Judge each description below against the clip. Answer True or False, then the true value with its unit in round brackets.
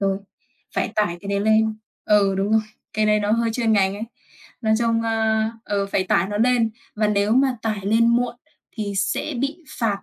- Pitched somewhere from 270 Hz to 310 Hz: False (215 Hz)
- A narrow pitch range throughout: True (2.1 semitones)